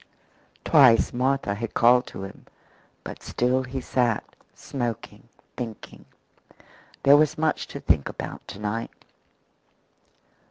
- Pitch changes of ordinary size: Yes, average, 3.0 semitones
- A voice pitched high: No, low, 125 Hz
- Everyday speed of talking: No, slow, 115 wpm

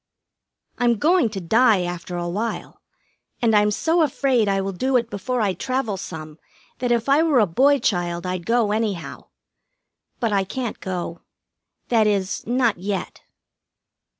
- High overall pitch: Yes, high, 215 Hz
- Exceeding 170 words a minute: No, average, 155 wpm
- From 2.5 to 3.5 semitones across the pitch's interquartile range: No, average, 5.0 semitones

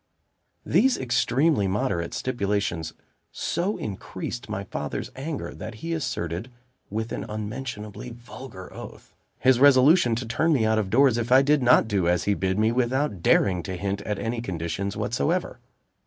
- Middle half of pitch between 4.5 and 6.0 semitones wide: Yes, average, 4.9 semitones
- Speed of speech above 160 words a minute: No, average, 155 wpm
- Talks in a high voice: No, low, 115 Hz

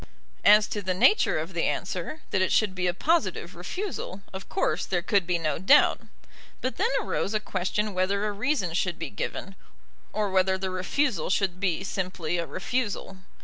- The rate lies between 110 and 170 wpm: No, average, 185 wpm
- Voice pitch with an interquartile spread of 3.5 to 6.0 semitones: No, narrow, 2.6 semitones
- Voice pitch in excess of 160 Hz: Yes, high, 190 Hz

